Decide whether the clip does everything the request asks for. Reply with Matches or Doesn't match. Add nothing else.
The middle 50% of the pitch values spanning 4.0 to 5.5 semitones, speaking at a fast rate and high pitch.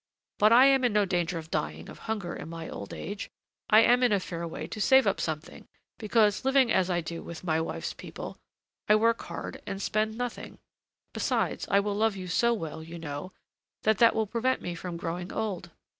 Matches